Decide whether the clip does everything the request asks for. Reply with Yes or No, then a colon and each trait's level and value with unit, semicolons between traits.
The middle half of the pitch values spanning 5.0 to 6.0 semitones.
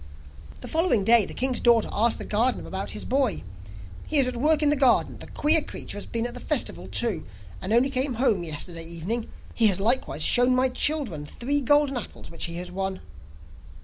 Yes: wide, 5.5 semitones